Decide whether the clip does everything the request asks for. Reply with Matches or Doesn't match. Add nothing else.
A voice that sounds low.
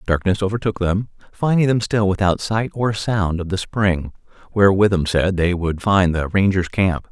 Matches